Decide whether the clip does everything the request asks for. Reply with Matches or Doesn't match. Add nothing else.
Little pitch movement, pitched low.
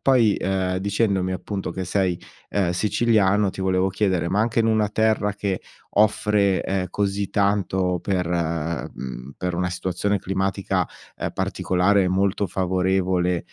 Matches